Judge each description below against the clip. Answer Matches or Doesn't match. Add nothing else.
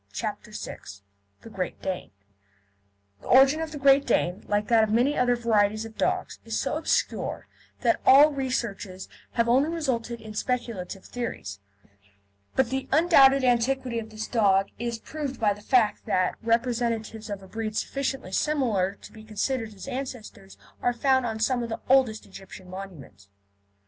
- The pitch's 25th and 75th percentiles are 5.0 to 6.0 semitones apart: Doesn't match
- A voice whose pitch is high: Matches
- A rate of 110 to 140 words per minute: Doesn't match